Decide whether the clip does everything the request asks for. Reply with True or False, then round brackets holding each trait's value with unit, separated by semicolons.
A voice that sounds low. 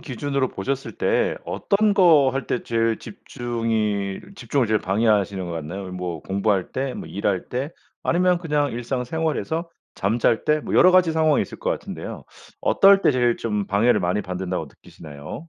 True (115 Hz)